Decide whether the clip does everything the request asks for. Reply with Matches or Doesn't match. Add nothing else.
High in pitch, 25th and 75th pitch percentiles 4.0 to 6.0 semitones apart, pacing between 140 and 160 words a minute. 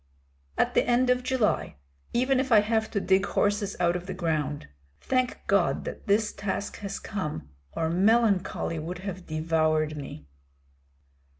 Matches